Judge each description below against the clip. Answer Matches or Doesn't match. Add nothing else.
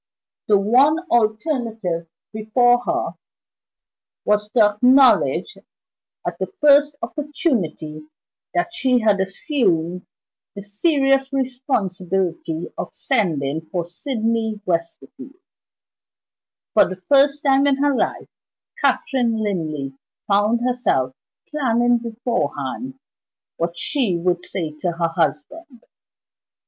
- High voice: Matches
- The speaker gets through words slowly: Matches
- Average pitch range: Doesn't match